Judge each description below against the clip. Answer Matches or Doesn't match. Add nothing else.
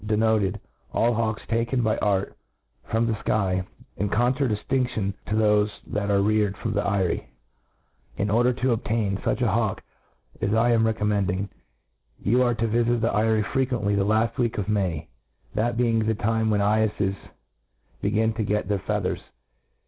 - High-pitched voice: Doesn't match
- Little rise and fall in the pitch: Matches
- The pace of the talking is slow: Doesn't match